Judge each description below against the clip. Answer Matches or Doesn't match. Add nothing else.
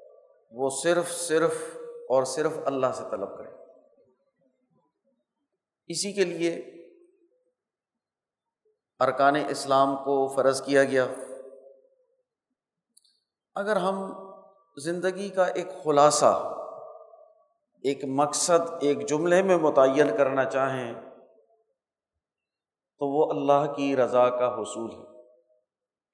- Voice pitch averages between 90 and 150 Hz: Doesn't match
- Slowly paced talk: Matches